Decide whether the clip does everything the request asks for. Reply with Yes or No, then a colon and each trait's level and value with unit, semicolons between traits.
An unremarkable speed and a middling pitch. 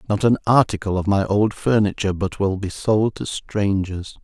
No: average, 185 wpm; low, 100 Hz